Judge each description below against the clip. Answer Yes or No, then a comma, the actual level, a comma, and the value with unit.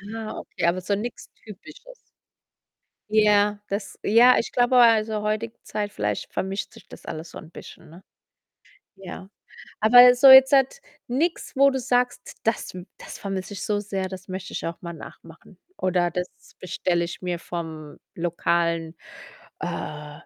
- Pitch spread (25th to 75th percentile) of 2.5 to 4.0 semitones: No, average, 5.0 semitones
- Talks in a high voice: Yes, high, 200 Hz